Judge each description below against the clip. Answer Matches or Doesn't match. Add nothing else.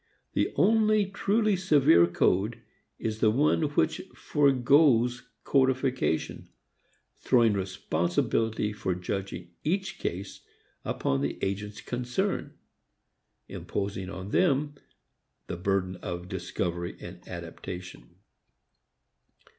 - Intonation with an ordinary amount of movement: Doesn't match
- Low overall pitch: Matches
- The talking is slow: Matches